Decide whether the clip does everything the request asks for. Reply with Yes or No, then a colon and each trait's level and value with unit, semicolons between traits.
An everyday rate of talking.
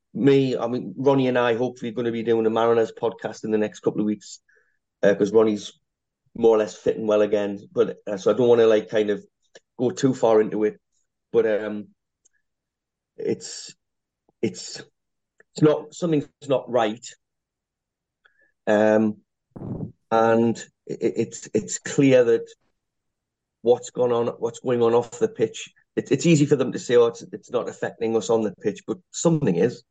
Yes: average, 180 wpm